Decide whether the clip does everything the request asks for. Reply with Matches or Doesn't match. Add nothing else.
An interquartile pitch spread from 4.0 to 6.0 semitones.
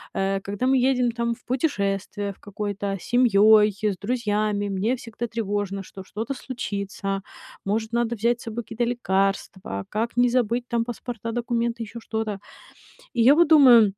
Doesn't match